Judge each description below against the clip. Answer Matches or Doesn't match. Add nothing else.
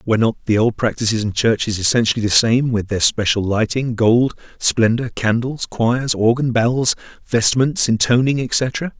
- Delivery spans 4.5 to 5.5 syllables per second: Matches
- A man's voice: Matches